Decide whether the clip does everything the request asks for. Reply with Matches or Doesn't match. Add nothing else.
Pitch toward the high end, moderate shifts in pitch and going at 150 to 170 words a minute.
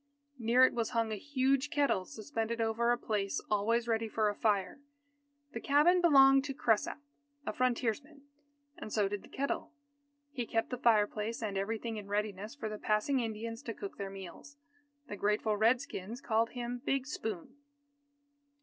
Matches